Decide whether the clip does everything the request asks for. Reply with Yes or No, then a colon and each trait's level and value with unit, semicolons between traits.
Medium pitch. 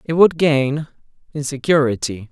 Yes: medium, 145 Hz